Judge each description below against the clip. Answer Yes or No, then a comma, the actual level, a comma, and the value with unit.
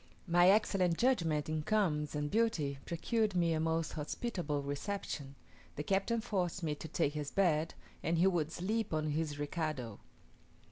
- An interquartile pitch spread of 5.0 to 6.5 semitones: No, average, 4.5 semitones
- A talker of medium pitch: Yes, medium, 165 Hz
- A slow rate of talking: No, average, 155 wpm